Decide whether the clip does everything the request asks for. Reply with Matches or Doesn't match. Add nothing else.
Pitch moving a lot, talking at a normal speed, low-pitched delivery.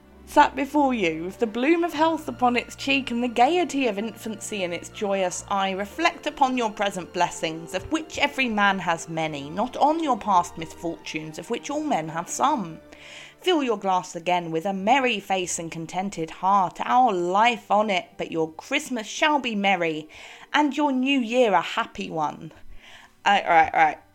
Doesn't match